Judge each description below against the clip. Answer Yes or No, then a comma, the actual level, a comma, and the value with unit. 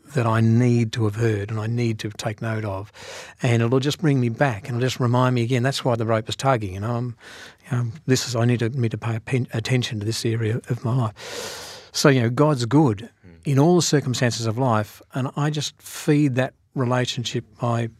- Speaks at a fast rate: Yes, fast, 235 wpm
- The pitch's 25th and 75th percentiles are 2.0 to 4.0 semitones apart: Yes, average, 2.9 semitones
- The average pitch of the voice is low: Yes, low, 120 Hz